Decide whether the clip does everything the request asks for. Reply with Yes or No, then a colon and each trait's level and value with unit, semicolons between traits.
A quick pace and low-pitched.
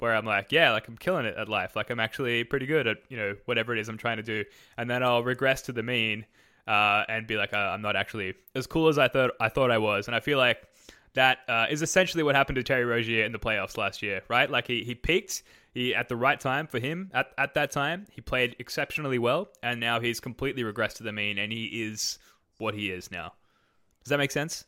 Yes: fast, 260 wpm; low, 120 Hz